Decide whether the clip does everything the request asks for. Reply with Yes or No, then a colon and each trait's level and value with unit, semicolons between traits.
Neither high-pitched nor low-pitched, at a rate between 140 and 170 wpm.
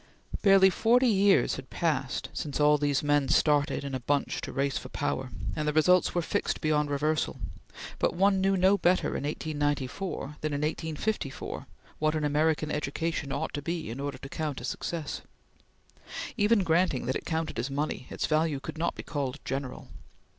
No: medium, 150 Hz; average, 180 wpm